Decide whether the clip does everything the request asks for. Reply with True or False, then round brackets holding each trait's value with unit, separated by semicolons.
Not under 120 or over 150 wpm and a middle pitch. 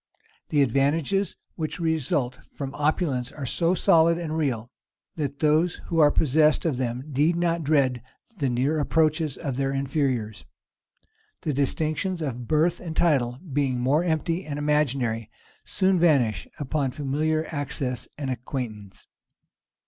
True (135 wpm; 145 Hz)